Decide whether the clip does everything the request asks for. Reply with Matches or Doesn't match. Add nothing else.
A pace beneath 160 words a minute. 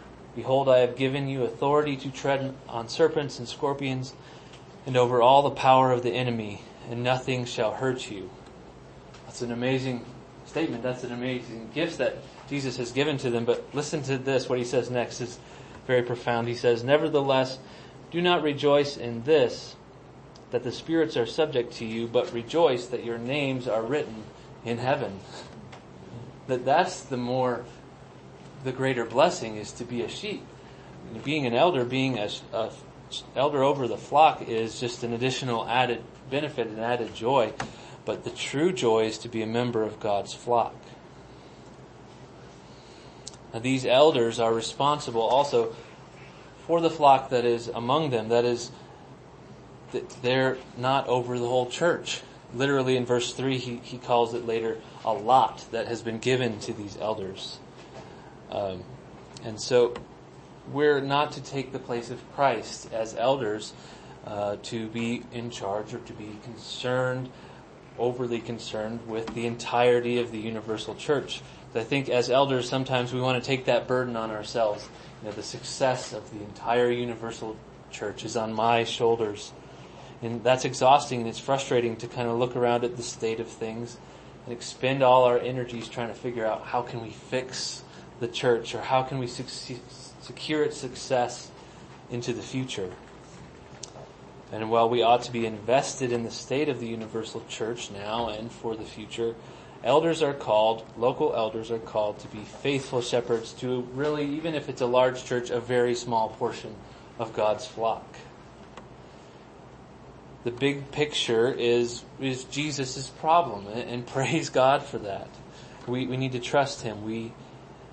Doesn't match